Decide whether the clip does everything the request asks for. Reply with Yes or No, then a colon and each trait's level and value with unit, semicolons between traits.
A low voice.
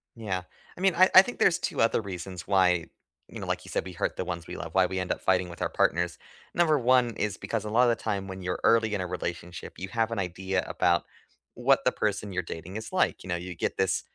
Yes: very low, 95 Hz